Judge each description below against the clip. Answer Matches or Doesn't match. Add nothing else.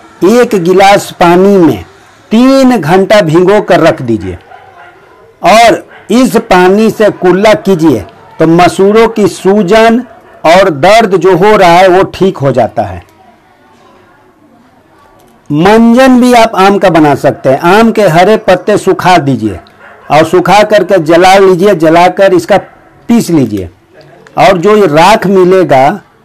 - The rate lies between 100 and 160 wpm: Matches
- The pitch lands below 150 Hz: Doesn't match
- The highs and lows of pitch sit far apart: Doesn't match